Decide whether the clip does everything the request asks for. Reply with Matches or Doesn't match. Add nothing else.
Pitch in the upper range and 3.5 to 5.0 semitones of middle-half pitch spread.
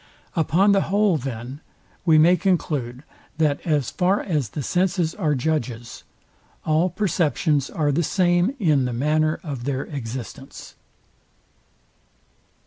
Doesn't match